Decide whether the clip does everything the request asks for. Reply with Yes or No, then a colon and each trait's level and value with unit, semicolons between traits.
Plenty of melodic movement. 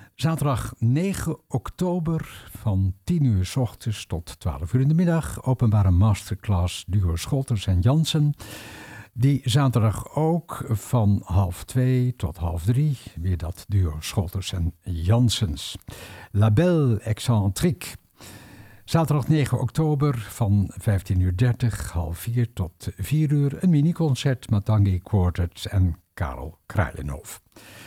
Yes: wide, 5.8 semitones